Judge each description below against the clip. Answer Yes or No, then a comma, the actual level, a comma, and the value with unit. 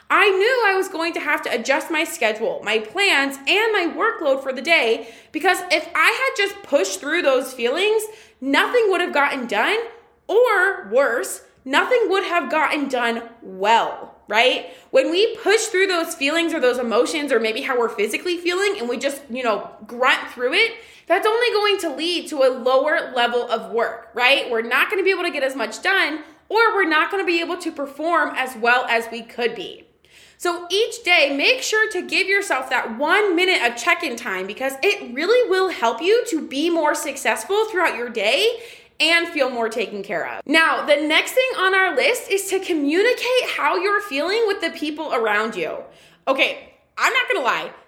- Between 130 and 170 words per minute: No, average, 200 wpm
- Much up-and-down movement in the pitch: Yes, wide, 7.4 semitones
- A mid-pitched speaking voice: No, very high, 330 Hz